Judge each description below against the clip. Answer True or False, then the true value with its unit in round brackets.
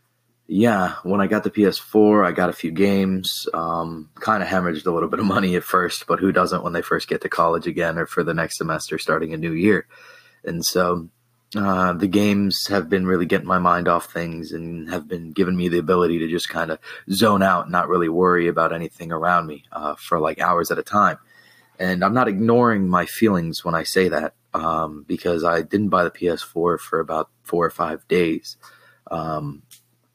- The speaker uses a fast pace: True (210 wpm)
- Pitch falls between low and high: False (90 Hz)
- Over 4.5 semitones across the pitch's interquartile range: False (2.8 semitones)